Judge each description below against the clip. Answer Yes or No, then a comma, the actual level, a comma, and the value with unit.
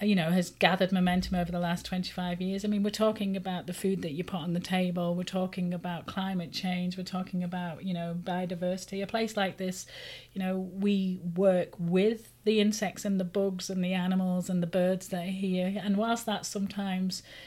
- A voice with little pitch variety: Yes, narrow, 1.5 semitones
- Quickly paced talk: Yes, fast, 210 wpm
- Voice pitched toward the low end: No, medium, 185 Hz